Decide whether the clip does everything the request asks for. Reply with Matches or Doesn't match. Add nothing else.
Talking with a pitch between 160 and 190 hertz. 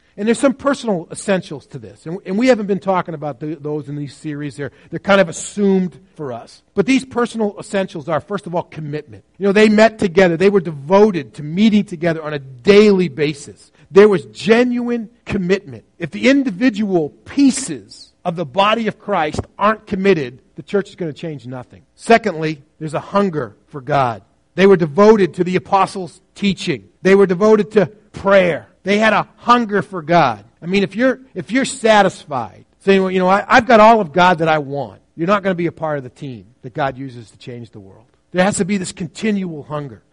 Matches